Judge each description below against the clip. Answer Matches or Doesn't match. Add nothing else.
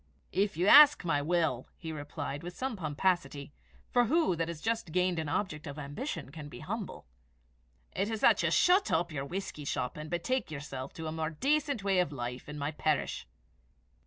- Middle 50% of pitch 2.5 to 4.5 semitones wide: Doesn't match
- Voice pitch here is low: Doesn't match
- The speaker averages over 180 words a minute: Matches